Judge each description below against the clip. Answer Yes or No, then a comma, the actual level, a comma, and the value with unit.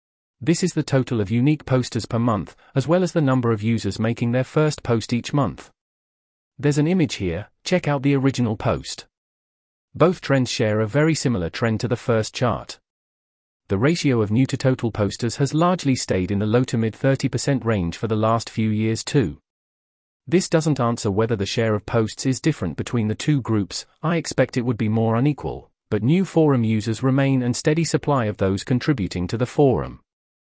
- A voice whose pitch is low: Yes, low, 120 Hz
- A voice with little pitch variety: No, average, 4.6 semitones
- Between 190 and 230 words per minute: Yes, average, 195 wpm